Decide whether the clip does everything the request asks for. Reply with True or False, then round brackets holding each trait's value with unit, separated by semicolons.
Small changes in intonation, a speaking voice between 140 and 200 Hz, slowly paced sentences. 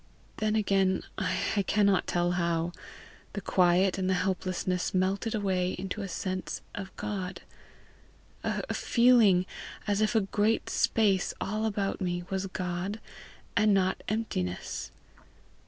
True (2.3 semitones; 190 Hz; 120 wpm)